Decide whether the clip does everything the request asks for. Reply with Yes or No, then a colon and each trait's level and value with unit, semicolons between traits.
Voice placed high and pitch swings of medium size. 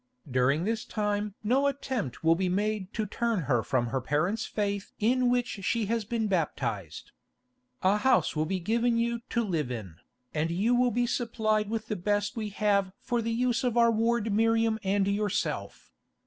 Yes: high, 210 Hz; average, 4.0 semitones